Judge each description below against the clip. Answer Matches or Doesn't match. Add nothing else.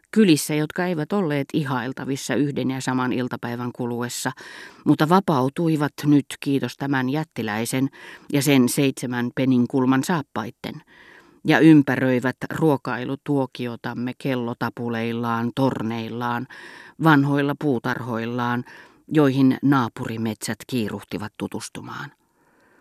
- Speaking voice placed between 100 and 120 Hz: Doesn't match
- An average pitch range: Matches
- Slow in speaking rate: Matches